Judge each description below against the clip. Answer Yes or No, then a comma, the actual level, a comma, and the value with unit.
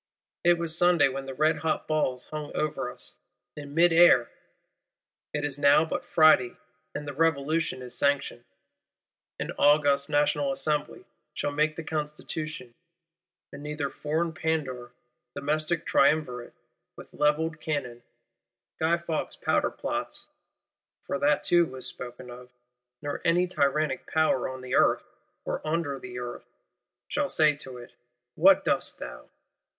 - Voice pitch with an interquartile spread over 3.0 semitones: No, average, 2.7 semitones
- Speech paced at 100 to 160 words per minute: Yes, average, 140 wpm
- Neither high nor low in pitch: Yes, medium, 150 Hz